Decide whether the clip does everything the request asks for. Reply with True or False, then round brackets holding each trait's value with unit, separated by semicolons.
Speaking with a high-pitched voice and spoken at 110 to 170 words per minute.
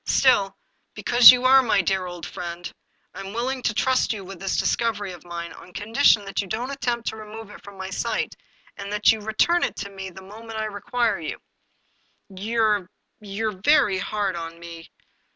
False (205 Hz; 205 wpm)